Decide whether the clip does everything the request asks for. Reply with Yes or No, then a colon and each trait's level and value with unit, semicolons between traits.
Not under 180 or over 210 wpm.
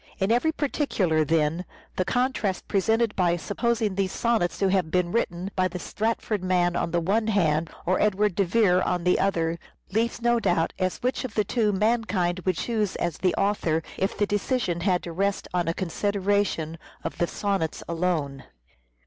Yes: average, 185 wpm